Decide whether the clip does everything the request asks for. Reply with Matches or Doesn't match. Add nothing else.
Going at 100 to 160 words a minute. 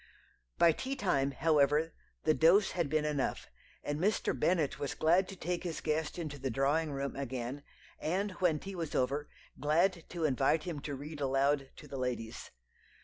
Doesn't match